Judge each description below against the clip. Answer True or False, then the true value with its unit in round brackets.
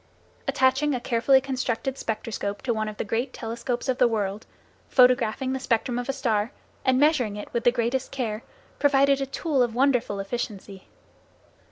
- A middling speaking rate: True (170 wpm)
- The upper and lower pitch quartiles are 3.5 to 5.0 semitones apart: False (3.1 semitones)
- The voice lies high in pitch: True (245 Hz)